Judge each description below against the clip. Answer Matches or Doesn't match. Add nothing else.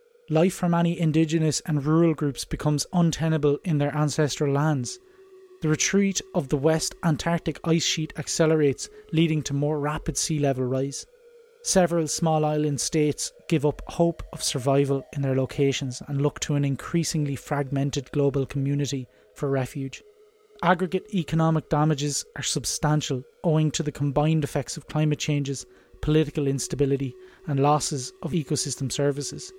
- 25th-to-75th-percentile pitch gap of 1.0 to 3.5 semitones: Matches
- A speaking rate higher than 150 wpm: Doesn't match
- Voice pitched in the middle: Matches